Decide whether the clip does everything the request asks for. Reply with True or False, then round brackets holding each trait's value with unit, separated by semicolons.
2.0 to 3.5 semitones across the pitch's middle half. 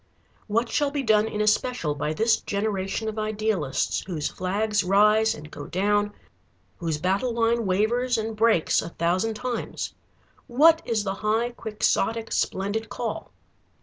True (3.0 semitones)